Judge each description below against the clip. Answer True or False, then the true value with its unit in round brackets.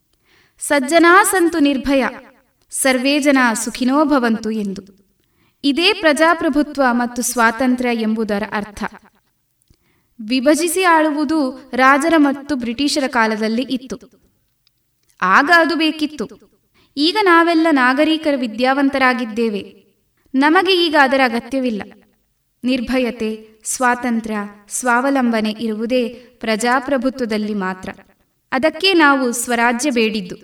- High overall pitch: True (255 Hz)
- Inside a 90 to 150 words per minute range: False (80 wpm)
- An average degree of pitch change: True (4.6 semitones)